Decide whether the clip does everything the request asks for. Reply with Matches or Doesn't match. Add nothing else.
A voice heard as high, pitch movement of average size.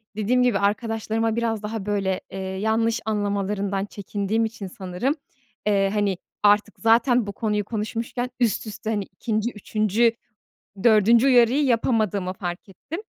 Doesn't match